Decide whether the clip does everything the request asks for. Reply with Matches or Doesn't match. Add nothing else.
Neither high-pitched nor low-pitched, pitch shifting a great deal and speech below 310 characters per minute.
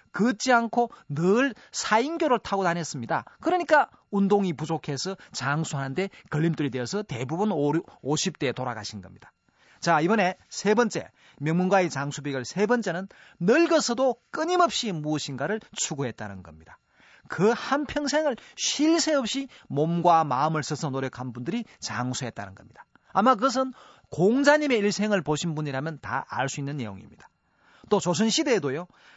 Doesn't match